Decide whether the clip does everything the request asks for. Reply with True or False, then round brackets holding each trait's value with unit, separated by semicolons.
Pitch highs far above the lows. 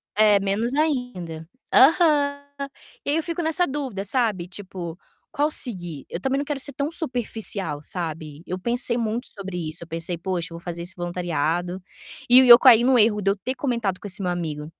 True (6.7 semitones)